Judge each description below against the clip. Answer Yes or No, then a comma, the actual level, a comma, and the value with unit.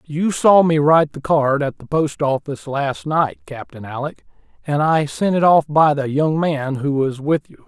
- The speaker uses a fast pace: Yes, fast, 210 wpm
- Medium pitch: Yes, medium, 145 Hz